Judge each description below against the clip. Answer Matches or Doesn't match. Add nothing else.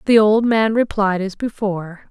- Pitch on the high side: Matches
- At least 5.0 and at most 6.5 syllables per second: Doesn't match